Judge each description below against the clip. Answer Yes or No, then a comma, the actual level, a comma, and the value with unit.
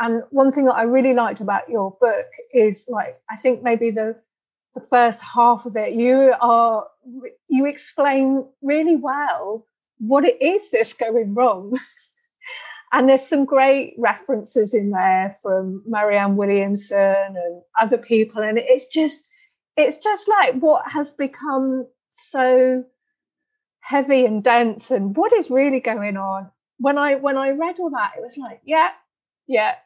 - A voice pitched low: No, very high, 255 Hz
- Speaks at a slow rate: No, average, 155 wpm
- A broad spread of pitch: No, average, 4.3 semitones